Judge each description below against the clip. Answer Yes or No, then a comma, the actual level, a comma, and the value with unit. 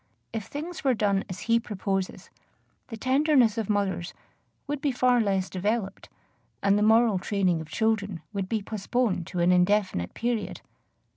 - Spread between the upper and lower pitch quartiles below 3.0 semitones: No, average, 3.6 semitones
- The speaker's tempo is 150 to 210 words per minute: Yes, average, 155 wpm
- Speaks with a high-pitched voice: Yes, high, 210 Hz